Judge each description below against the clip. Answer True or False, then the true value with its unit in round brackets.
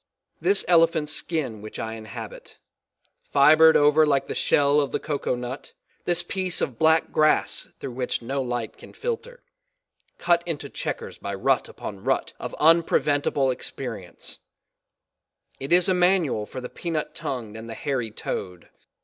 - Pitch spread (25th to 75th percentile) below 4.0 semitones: False (5.2 semitones)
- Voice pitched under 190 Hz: True (140 Hz)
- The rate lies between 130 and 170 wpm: True (150 wpm)